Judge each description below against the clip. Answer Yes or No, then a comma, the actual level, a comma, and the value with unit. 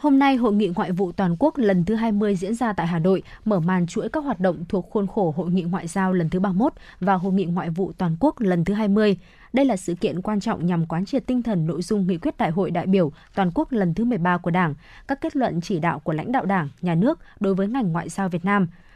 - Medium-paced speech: No, fast, 270 wpm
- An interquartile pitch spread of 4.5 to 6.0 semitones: No, average, 3.4 semitones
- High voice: Yes, high, 195 Hz